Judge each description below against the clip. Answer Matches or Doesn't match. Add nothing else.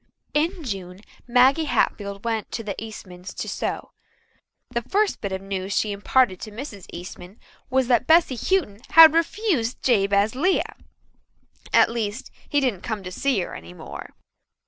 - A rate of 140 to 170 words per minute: Matches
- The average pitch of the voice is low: Doesn't match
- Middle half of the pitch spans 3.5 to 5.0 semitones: Doesn't match